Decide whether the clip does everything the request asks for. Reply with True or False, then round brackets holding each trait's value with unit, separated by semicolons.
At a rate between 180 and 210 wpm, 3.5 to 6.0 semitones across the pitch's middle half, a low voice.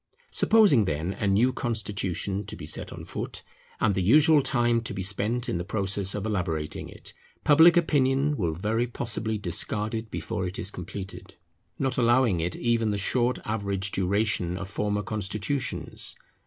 False (165 wpm; 3.9 semitones; 105 Hz)